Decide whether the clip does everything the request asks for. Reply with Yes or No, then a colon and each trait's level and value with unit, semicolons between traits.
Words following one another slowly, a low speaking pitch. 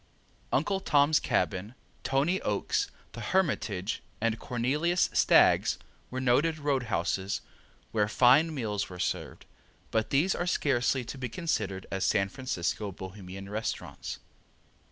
Yes: slow, 125 wpm; low, 120 Hz